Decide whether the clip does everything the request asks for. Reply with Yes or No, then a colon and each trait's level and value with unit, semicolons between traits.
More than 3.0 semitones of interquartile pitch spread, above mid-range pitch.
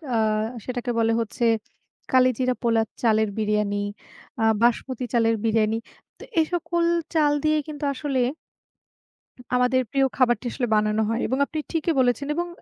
Yes: average, 3.6 semitones; high, 245 Hz